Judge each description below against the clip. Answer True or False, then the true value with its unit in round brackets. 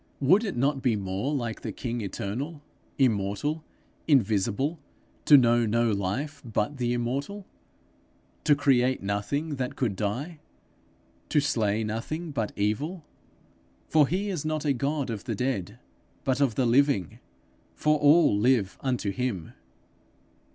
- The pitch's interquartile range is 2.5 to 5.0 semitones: False (5.4 semitones)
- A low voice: True (130 Hz)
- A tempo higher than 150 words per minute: False (135 wpm)